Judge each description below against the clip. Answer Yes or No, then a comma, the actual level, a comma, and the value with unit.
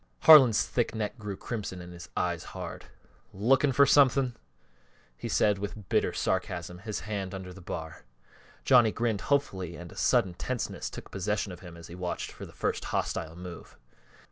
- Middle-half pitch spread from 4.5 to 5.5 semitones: Yes, average, 5.0 semitones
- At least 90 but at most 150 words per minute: No, average, 170 wpm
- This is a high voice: No, low, 100 Hz